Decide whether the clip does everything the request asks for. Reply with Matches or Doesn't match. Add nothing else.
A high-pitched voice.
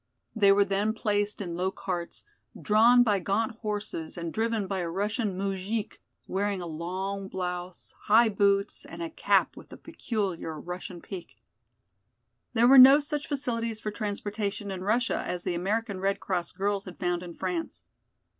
Matches